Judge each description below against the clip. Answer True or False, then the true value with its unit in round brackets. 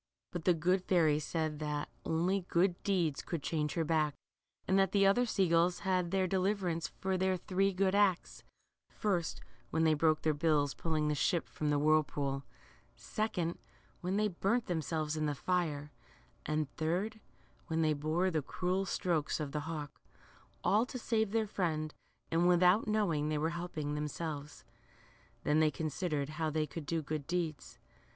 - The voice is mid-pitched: True (165 Hz)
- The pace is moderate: True (170 wpm)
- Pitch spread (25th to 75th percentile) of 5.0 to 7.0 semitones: False (3.4 semitones)